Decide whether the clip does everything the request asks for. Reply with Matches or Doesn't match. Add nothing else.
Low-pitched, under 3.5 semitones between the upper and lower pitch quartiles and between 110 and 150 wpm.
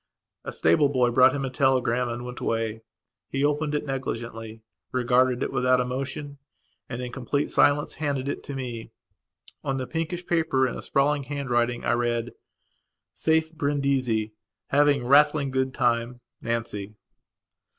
Matches